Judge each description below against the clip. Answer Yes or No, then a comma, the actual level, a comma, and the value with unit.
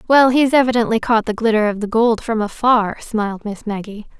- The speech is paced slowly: No, average, 200 wpm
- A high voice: Yes, high, 225 Hz